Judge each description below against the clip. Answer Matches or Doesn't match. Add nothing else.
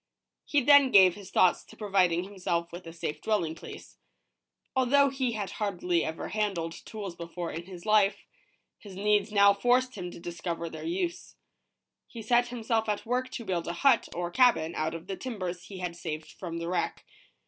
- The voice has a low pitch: Doesn't match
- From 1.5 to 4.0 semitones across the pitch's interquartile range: Doesn't match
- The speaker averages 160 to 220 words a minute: Matches